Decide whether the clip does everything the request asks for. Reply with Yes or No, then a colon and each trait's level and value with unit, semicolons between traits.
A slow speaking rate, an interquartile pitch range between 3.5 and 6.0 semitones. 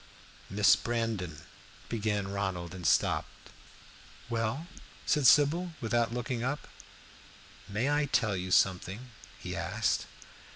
Yes: slow, 110 wpm; average, 4.8 semitones